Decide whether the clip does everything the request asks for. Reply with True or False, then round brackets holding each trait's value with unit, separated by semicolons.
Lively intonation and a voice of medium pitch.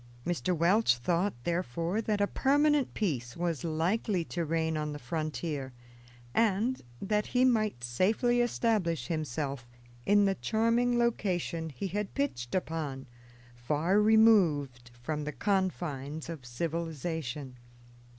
True (6.1 semitones; 170 Hz)